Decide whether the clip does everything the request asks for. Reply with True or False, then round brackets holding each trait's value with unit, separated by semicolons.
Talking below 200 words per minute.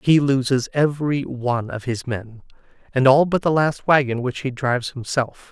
True (185 wpm)